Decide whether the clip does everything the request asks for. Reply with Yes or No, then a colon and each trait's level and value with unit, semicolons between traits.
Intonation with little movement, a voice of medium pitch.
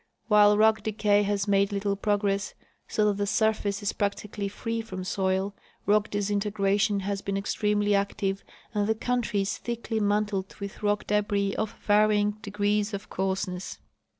No: narrow, 1.0 semitones; high, 205 Hz